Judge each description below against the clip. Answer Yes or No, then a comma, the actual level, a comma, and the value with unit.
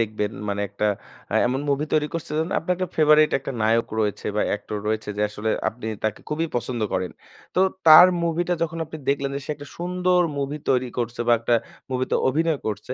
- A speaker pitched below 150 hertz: Yes, low, 135 Hz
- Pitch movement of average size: No, wide, 6.4 semitones